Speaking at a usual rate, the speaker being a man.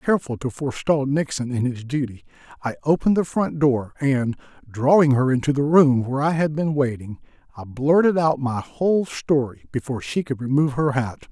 Yes: average, 185 wpm; male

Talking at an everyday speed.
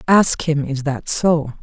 Yes: average, 185 wpm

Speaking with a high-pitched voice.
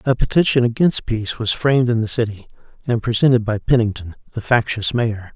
No: low, 115 Hz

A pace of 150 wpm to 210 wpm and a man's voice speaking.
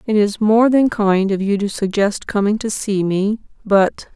No: average, 200 wpm; female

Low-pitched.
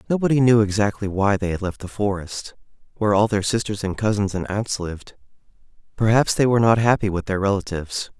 Yes: low, 105 Hz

